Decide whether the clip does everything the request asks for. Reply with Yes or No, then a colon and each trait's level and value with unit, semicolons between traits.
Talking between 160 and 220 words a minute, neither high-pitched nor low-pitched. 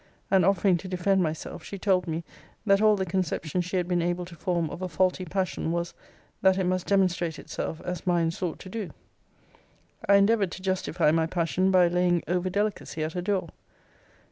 Yes: average, 195 wpm; medium, 180 Hz